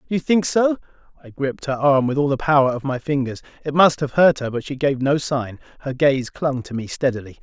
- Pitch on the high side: No, medium, 140 Hz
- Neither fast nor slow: No, fast, 250 wpm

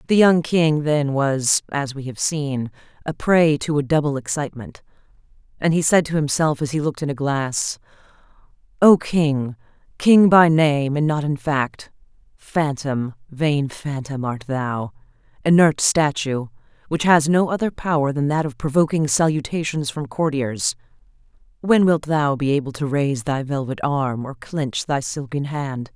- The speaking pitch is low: No, medium, 145 Hz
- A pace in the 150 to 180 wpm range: Yes, average, 155 wpm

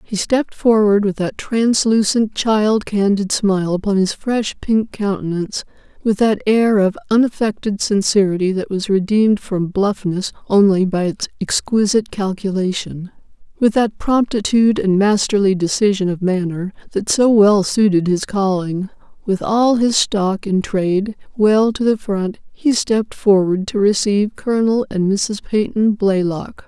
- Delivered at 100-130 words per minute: No, average, 140 wpm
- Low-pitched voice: No, high, 205 Hz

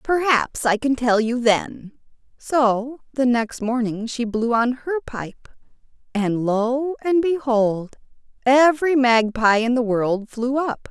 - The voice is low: No, high, 245 Hz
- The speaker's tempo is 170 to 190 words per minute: No, average, 145 wpm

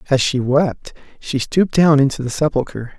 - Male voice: Yes, male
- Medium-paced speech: Yes, average, 180 wpm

